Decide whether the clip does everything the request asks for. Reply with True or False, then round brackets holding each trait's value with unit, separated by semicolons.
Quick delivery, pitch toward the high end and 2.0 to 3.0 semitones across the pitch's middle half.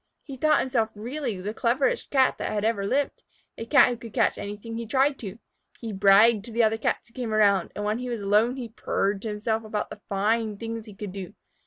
True (230 wpm; 220 Hz; 2.5 semitones)